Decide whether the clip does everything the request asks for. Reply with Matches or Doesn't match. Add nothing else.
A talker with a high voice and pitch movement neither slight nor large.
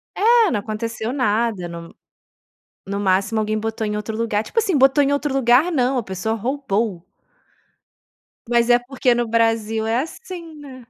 Matches